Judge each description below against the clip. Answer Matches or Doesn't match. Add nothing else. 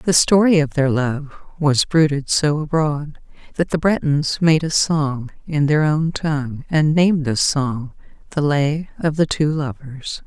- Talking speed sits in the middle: Matches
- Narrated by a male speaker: Doesn't match